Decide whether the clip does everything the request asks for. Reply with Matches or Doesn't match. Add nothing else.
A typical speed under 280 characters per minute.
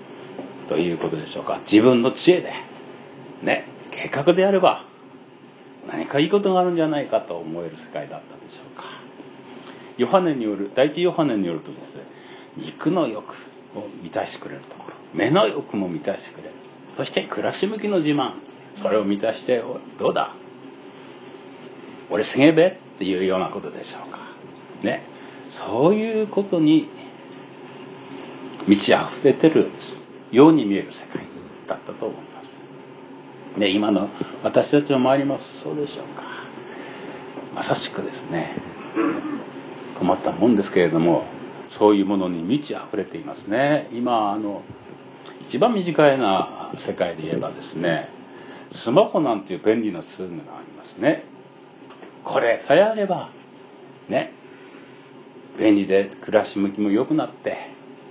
Doesn't match